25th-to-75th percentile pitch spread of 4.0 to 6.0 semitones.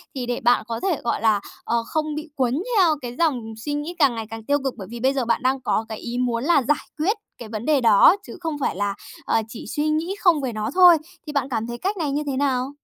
Yes: average, 4.7 semitones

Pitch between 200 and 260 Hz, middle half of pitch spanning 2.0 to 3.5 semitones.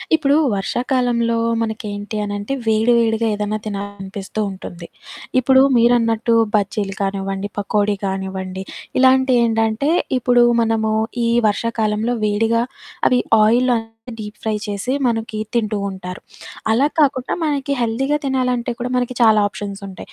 Yes: high, 220 Hz; average, 3.1 semitones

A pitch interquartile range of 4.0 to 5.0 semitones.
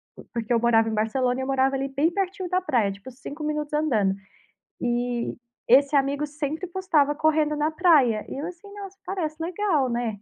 Yes: average, 4.6 semitones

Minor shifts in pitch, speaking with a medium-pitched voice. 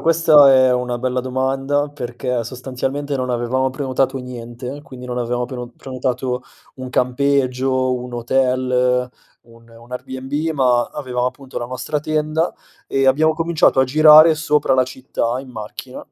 No: narrow, 2.0 semitones; low, 130 Hz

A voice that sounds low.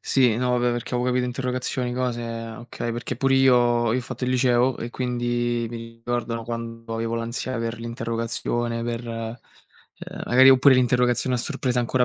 Yes: low, 120 Hz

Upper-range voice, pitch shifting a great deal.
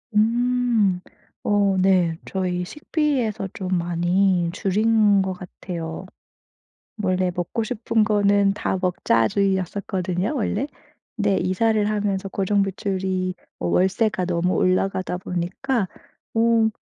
No: high, 195 Hz; average, 2.7 semitones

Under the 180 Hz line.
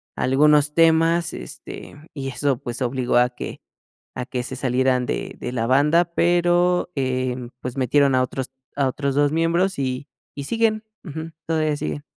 Yes: medium, 140 Hz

